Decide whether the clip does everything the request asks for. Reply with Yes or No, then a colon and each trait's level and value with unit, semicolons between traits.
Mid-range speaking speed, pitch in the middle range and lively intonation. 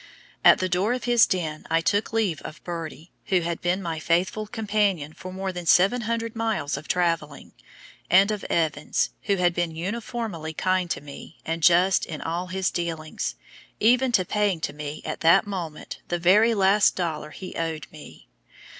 No: average, 175 wpm; medium, 180 Hz; average, 3.9 semitones